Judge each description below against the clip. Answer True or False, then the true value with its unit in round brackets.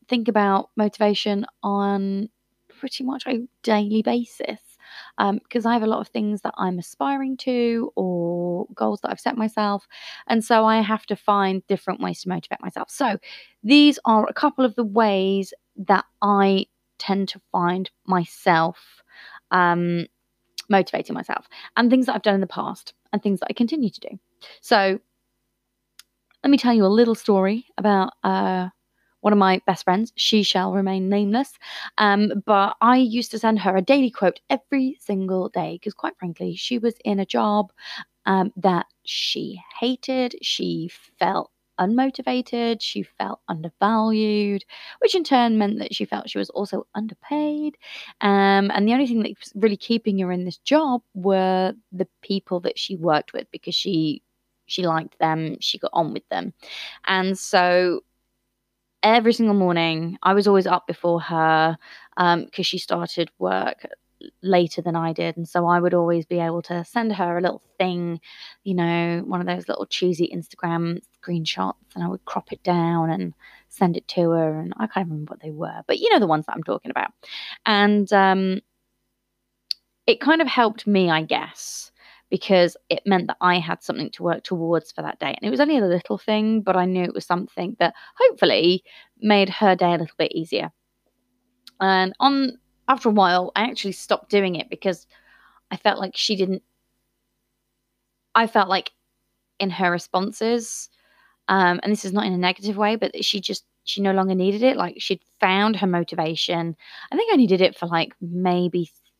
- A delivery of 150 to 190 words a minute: True (180 wpm)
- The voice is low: False (195 Hz)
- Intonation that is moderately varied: True (4.0 semitones)